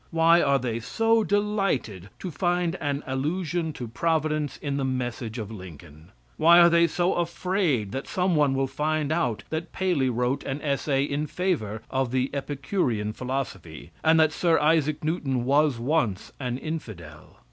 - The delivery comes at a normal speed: Yes, average, 160 wpm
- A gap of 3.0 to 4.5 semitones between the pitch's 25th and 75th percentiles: No, average, 5.0 semitones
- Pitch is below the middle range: No, medium, 145 Hz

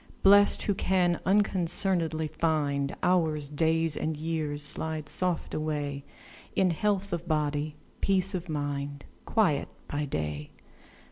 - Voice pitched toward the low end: No, medium, 160 Hz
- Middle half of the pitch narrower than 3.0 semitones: No, average, 3.7 semitones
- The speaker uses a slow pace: Yes, slow, 120 wpm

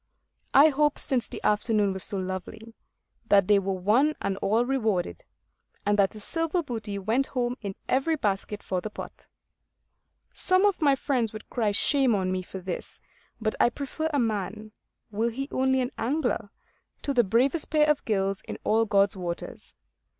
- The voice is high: Yes, high, 225 Hz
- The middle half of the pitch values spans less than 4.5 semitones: No, wide, 5.4 semitones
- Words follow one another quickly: No, average, 175 wpm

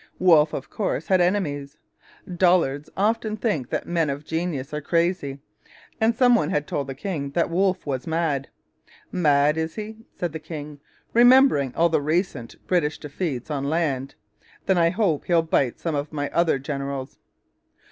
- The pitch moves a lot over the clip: No, average, 4.2 semitones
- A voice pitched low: No, medium, 160 Hz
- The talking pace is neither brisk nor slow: Yes, average, 165 wpm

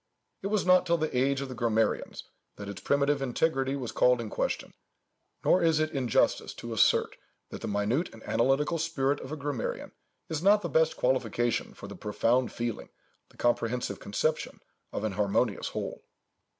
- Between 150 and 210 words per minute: Yes, average, 175 wpm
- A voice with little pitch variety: No, average, 5.1 semitones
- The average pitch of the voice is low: Yes, low, 130 Hz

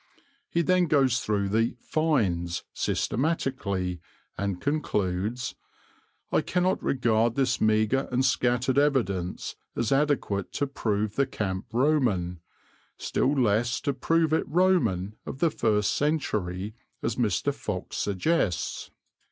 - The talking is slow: Yes, slow, 120 wpm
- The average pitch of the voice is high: No, low, 120 Hz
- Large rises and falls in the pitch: Yes, wide, 6.0 semitones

